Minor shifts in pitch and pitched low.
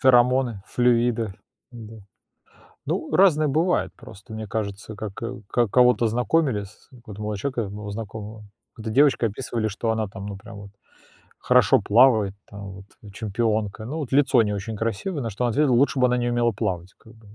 No: average, 3.1 semitones; low, 115 Hz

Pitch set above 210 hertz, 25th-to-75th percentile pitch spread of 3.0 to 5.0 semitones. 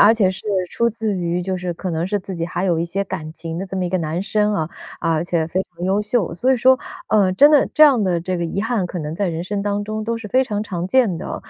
No: high, 190 Hz; average, 3.8 semitones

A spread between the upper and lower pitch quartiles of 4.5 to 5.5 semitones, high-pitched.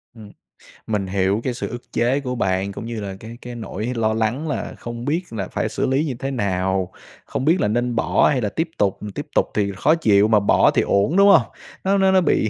No: average, 4.9 semitones; low, 115 Hz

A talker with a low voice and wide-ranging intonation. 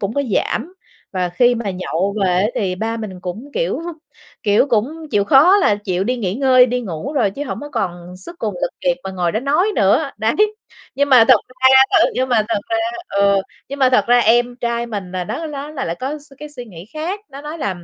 No: high, 235 Hz; wide, 6.0 semitones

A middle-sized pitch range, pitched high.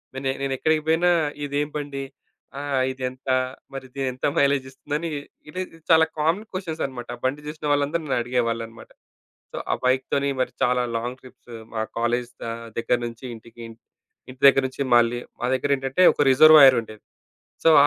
No: average, 3.0 semitones; low, 135 Hz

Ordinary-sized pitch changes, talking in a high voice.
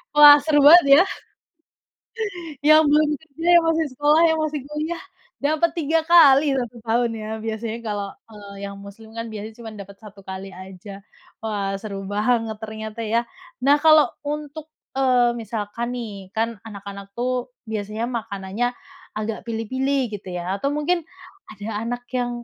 No: wide, 5.7 semitones; high, 230 Hz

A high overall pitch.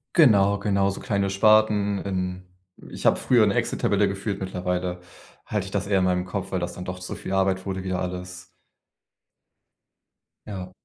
No: very low, 95 Hz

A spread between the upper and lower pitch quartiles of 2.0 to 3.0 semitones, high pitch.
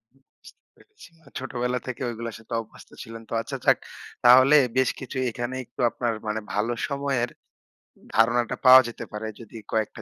No: narrow, 2.4 semitones; low, 120 Hz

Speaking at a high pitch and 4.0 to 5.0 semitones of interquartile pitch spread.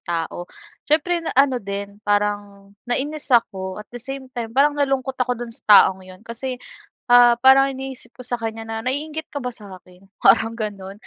Yes: high, 235 Hz; average, 4.7 semitones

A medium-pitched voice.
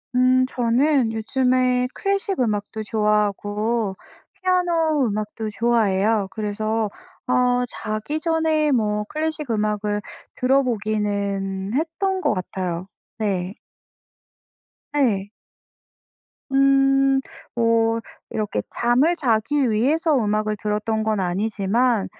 No: high, 225 Hz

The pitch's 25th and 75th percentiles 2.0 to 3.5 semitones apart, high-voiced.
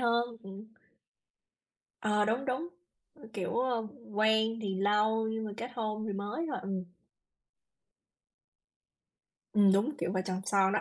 Yes: narrow, 2.6 semitones; high, 215 Hz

